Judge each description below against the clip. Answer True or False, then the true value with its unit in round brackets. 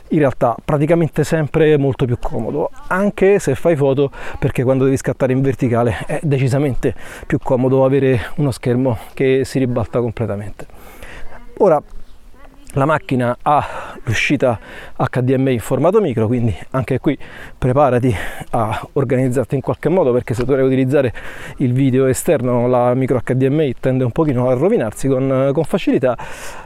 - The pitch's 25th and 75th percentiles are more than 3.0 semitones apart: False (2.6 semitones)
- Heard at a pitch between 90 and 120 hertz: False (135 Hz)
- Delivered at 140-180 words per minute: True (145 wpm)